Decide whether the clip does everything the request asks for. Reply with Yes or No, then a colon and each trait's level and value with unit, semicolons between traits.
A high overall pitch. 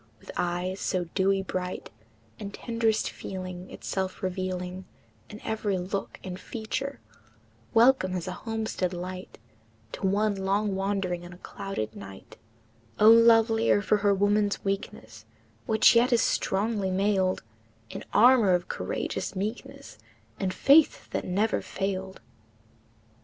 Yes: high, 195 Hz